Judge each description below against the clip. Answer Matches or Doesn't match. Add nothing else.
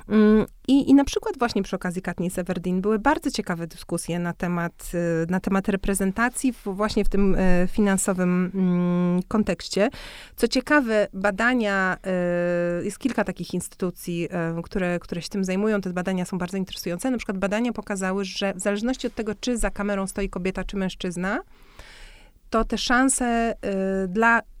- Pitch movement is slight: Doesn't match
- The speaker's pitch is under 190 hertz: Doesn't match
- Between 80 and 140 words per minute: Doesn't match